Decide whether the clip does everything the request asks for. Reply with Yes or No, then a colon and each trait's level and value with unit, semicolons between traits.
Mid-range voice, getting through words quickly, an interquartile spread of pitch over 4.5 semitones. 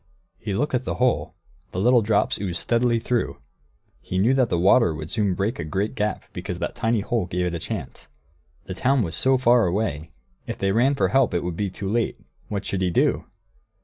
No: low, 105 Hz; fast, 215 wpm; average, 4.9 semitones